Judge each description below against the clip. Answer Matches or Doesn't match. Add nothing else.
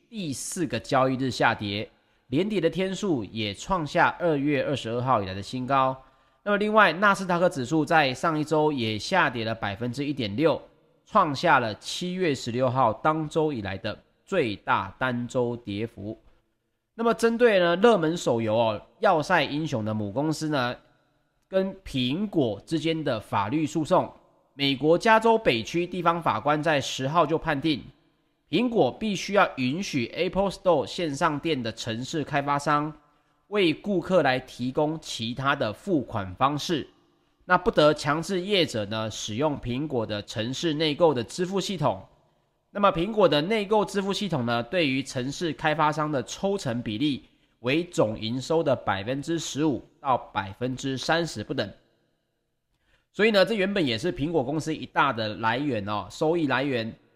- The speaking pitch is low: Doesn't match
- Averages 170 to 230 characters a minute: Doesn't match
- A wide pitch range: Matches